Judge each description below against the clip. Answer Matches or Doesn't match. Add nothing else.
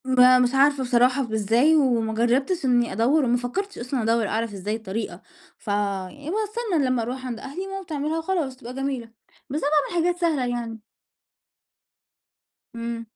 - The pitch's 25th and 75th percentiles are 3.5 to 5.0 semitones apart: Matches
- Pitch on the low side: Doesn't match